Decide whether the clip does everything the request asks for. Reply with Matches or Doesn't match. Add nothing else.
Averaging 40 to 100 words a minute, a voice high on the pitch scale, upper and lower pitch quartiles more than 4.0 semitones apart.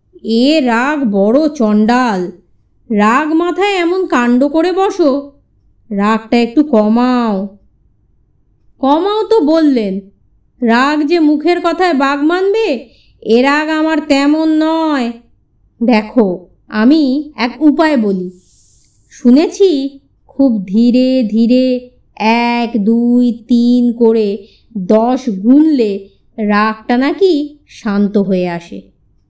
Matches